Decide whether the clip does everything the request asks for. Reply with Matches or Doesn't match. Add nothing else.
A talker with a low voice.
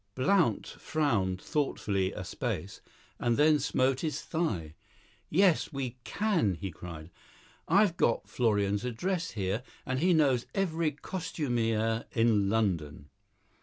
Matches